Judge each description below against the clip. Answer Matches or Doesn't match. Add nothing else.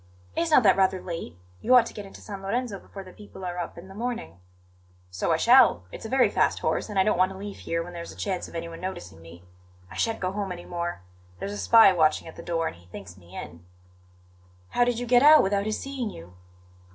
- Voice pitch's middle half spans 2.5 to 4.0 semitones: Doesn't match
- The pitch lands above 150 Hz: Matches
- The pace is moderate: Doesn't match